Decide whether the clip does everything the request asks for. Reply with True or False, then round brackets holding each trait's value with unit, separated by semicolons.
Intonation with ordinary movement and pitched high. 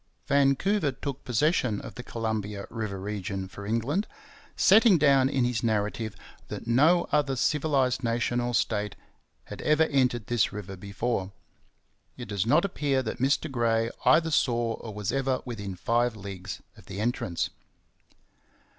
False (4.7 semitones; 120 Hz)